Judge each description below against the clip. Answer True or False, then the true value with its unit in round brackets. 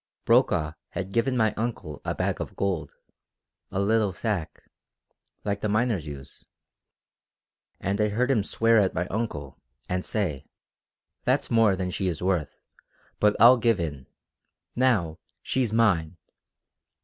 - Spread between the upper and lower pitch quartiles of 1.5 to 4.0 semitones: False (5.0 semitones)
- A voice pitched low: True (100 Hz)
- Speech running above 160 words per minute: False (135 wpm)